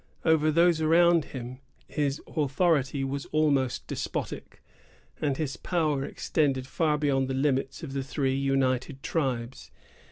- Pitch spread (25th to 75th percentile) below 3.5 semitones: Yes, average, 2.7 semitones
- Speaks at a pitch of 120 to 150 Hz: Yes, medium, 140 Hz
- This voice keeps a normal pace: No, slow, 130 wpm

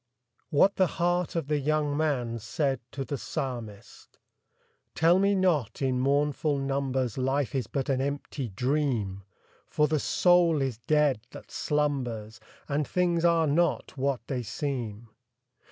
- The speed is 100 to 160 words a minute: Yes, average, 140 wpm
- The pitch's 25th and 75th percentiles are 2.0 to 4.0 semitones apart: Yes, average, 3.3 semitones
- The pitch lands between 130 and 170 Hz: Yes, medium, 140 Hz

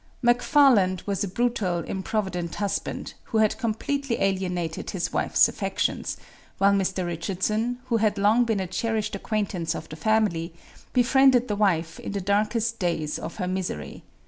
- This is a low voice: No, high, 200 Hz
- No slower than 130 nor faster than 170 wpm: Yes, average, 150 wpm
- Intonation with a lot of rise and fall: No, average, 3.9 semitones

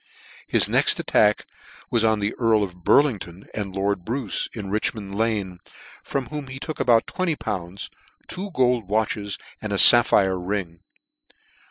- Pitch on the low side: Yes, low, 105 Hz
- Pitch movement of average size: Yes, average, 3.7 semitones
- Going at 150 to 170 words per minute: Yes, average, 155 wpm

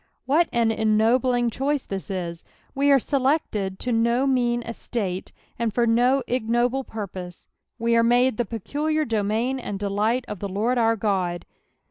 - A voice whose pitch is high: Yes, high, 235 Hz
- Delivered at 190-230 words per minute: No, average, 165 wpm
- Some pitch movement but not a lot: Yes, average, 3.4 semitones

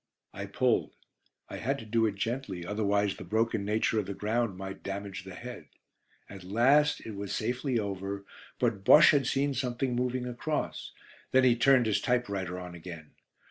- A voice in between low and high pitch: No, low, 110 Hz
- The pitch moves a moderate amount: Yes, average, 4.1 semitones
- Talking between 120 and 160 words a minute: No, average, 175 wpm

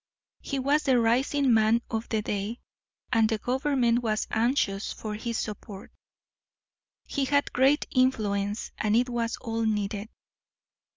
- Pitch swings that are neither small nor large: Yes, average, 3.2 semitones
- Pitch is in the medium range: No, high, 230 Hz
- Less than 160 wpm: Yes, slow, 135 wpm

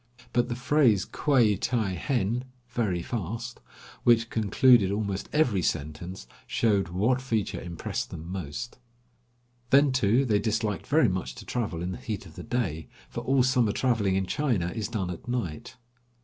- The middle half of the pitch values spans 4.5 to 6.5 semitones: Yes, average, 4.9 semitones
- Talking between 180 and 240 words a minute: No, average, 160 wpm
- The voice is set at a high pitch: No, low, 110 Hz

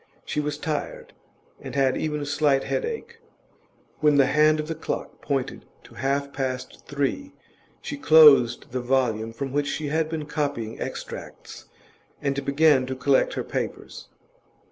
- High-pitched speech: No, medium, 145 Hz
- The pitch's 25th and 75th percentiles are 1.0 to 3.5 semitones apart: Yes, narrow, 2.5 semitones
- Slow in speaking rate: No, average, 150 wpm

